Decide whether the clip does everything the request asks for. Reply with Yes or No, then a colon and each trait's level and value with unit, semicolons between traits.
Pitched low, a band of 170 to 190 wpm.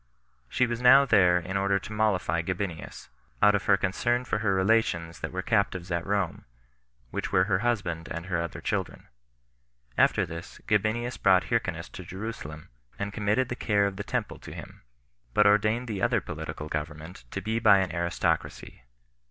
Yes: low, 100 Hz; average, 175 wpm